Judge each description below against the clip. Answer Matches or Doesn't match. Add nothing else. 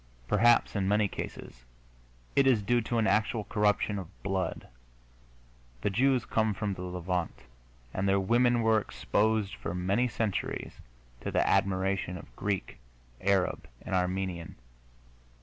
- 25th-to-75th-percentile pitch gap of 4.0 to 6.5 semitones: Doesn't match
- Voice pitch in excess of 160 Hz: Doesn't match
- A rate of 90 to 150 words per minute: Matches